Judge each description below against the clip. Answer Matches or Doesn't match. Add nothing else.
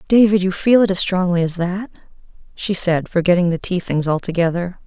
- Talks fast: Doesn't match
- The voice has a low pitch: Doesn't match